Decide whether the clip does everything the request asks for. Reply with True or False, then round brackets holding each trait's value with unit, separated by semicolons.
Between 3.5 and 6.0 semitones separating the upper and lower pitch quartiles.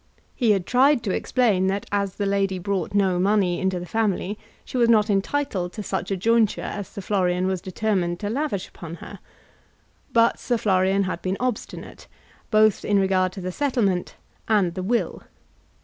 False (2.9 semitones)